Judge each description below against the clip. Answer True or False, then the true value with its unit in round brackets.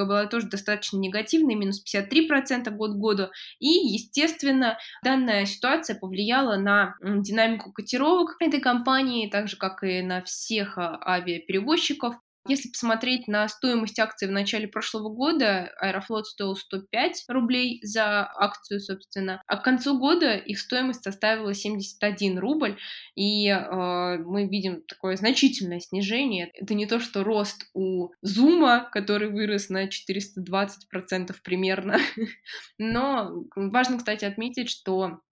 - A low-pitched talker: False (210 Hz)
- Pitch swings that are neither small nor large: True (4.1 semitones)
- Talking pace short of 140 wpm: True (125 wpm)